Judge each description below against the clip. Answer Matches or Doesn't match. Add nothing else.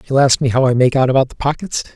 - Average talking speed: Doesn't match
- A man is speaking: Matches